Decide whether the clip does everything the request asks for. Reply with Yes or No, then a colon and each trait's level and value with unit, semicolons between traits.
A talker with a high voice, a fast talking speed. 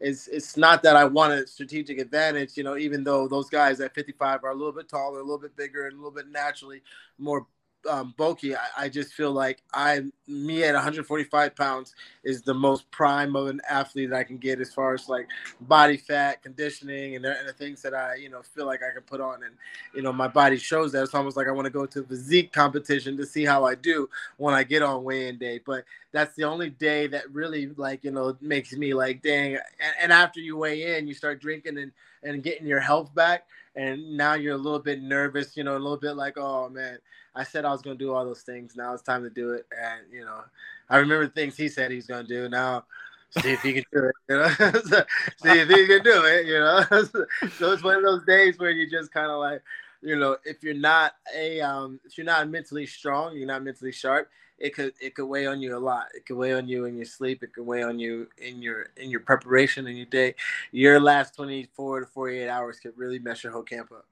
No: medium, 140 Hz; fast, 250 wpm